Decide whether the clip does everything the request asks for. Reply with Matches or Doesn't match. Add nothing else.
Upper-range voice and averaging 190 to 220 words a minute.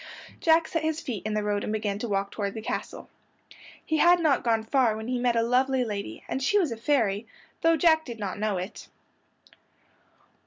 Matches